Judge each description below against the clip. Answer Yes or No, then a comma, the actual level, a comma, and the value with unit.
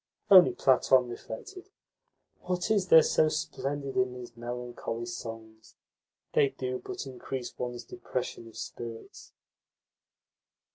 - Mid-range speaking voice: No, low, 125 Hz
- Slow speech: Yes, slow, 110 wpm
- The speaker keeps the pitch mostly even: No, average, 3.3 semitones